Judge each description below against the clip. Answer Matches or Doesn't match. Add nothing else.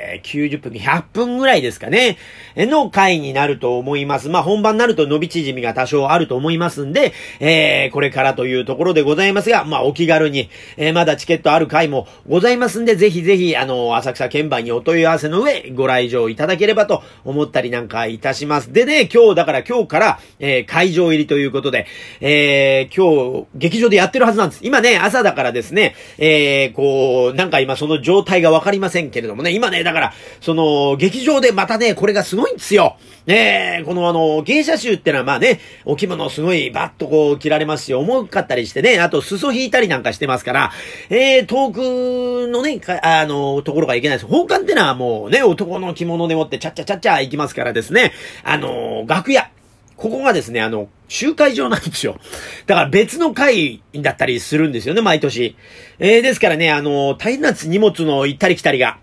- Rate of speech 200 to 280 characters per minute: Doesn't match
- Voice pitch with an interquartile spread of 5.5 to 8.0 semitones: Matches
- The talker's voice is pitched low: Doesn't match